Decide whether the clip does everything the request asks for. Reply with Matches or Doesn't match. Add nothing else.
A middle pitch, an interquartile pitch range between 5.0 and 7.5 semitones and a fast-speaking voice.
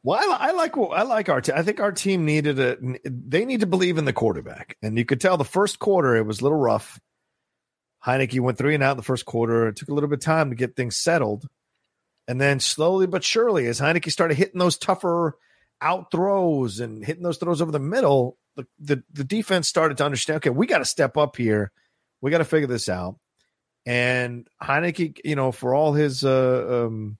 Matches